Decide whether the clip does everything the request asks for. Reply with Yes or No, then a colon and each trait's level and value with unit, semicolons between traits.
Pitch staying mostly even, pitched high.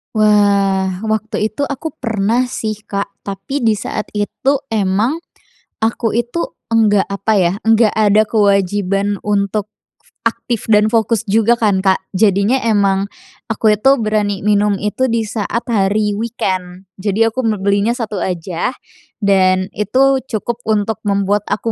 Yes: narrow, 2.3 semitones; high, 210 Hz